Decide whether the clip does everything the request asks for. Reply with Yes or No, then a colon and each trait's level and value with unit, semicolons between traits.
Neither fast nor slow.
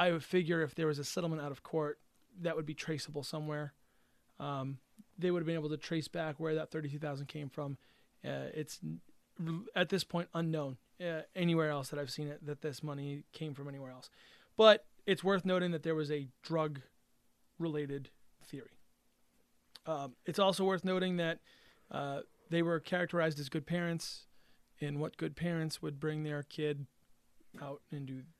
Yes: average, 180 wpm